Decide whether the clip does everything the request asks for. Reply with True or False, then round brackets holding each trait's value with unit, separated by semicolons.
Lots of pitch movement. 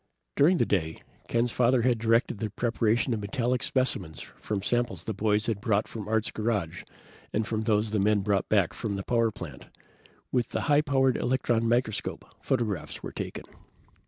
False (2.8 semitones)